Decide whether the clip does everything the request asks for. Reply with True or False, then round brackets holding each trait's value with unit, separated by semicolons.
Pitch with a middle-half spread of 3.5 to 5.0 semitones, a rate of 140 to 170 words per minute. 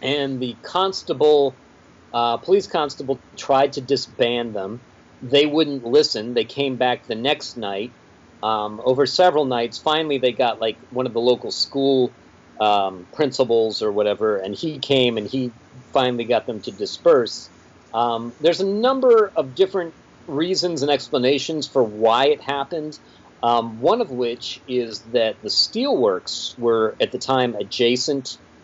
True (4.3 semitones; 150 wpm)